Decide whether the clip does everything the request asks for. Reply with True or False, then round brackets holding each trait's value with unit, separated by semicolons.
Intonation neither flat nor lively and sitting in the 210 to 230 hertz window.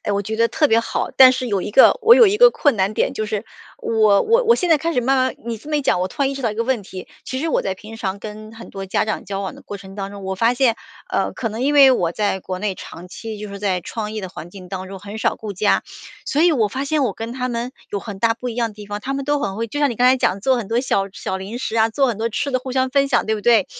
True (4.6 semitones; 225 Hz)